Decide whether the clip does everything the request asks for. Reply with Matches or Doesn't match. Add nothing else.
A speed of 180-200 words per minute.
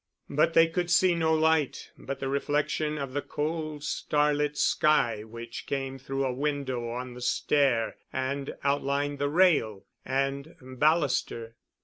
Doesn't match